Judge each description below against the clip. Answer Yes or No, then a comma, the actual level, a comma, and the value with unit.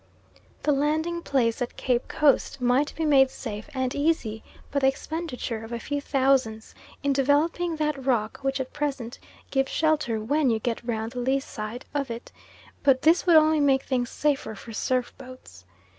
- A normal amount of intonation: Yes, average, 3.5 semitones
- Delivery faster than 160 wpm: Yes, average, 175 wpm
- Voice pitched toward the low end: No, very high, 270 Hz